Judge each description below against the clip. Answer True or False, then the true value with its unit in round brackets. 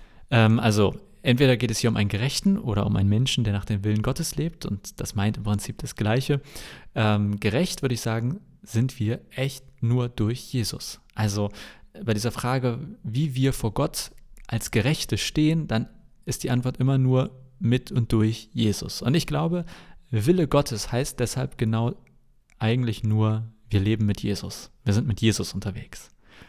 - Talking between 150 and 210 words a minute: True (170 wpm)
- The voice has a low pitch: True (120 Hz)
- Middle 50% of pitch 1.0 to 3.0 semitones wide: False (3.6 semitones)